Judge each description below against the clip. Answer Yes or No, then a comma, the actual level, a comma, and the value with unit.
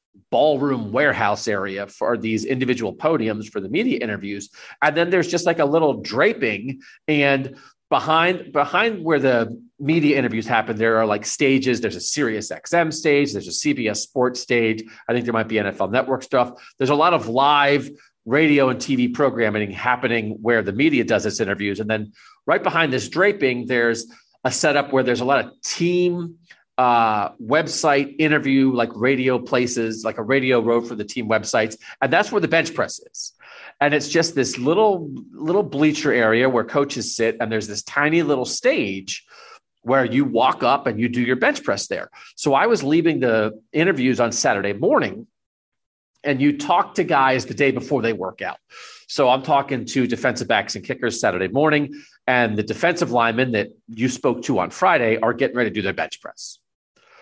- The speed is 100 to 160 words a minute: No, average, 185 wpm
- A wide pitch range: No, average, 4.3 semitones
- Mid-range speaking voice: No, low, 130 Hz